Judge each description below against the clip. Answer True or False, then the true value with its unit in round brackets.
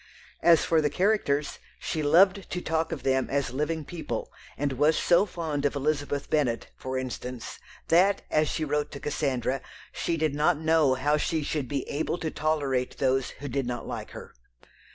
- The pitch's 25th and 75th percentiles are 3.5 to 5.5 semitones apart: False (2.9 semitones)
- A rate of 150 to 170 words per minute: False (180 wpm)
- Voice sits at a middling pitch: True (150 Hz)